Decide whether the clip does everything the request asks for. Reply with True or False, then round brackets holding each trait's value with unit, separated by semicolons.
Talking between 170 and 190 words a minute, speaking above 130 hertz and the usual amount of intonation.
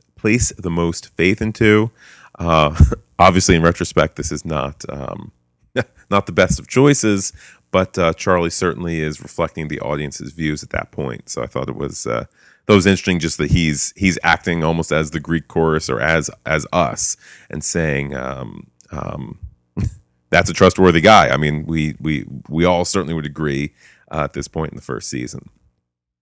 False (180 wpm; 80 Hz; 4.0 semitones)